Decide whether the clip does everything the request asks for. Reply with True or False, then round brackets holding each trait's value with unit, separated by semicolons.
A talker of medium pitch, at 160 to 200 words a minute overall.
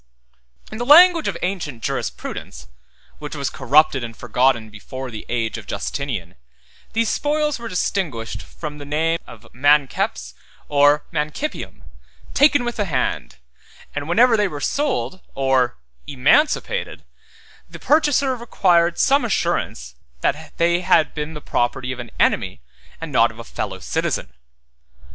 False (150 Hz; 140 wpm)